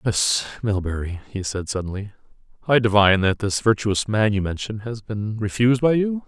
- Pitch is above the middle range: No, low, 105 Hz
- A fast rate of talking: No, average, 170 wpm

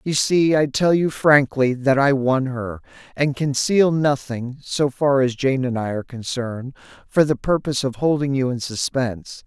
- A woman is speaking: No, male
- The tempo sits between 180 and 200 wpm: Yes, average, 185 wpm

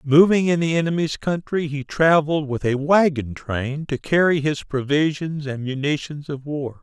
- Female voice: No, male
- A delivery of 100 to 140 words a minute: No, average, 165 wpm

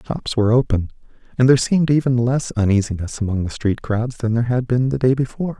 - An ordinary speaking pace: No, fast, 215 wpm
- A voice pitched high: No, low, 120 Hz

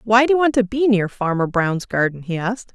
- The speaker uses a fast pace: Yes, fast, 260 wpm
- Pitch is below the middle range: No, high, 210 Hz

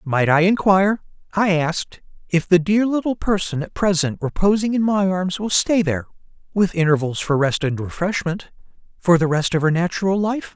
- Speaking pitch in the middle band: Yes, medium, 180 Hz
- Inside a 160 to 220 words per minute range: Yes, average, 180 wpm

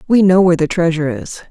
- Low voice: No, medium, 175 Hz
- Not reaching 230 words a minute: No, fast, 240 wpm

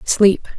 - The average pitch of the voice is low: No, high, 200 Hz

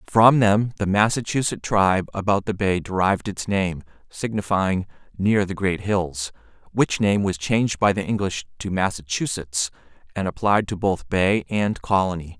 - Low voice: Yes, low, 100 Hz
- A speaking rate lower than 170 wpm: Yes, average, 155 wpm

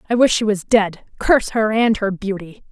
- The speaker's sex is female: Yes, female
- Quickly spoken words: Yes, fast, 220 wpm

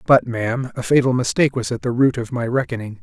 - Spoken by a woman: No, male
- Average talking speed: No, fast, 240 wpm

